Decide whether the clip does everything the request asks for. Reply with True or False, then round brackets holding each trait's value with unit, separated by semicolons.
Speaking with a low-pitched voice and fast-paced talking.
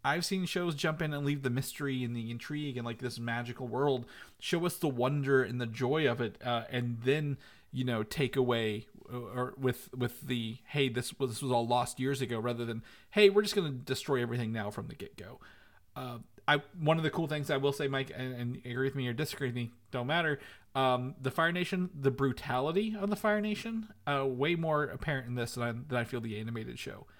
True (130 Hz; 230 wpm)